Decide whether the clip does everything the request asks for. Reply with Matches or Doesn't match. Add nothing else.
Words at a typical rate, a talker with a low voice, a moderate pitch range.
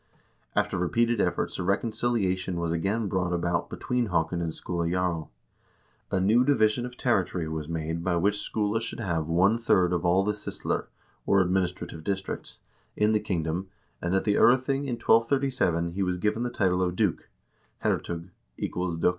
Matches